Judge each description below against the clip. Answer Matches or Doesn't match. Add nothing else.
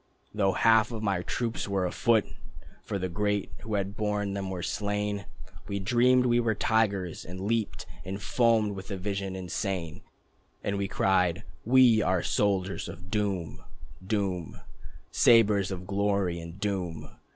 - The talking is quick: Doesn't match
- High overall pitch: Doesn't match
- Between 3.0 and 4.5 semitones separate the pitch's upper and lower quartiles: Doesn't match